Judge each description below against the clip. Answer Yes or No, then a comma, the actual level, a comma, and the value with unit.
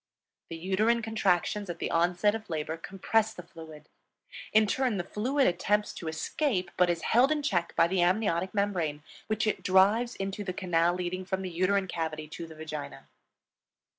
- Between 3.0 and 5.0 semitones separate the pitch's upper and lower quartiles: Yes, average, 3.8 semitones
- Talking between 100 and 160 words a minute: No, average, 175 wpm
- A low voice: No, medium, 185 Hz